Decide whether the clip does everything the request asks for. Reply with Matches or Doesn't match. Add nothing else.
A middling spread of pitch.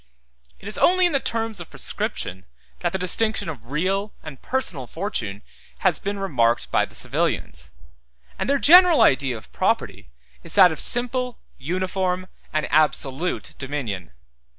Doesn't match